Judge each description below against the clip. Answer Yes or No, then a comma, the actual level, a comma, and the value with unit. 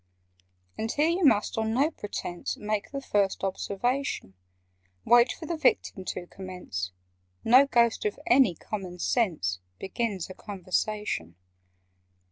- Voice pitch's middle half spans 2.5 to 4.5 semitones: No, average, 5.1 semitones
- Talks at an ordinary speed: No, slow, 125 wpm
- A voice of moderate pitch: No, high, 210 Hz